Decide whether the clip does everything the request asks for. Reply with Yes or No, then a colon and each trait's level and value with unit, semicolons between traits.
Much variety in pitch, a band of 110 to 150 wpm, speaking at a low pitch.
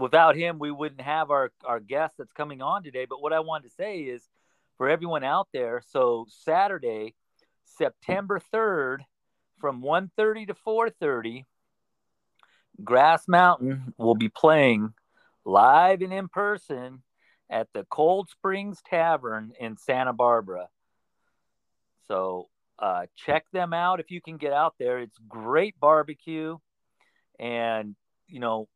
No: wide, 7.3 semitones; average, 140 wpm; medium, 155 Hz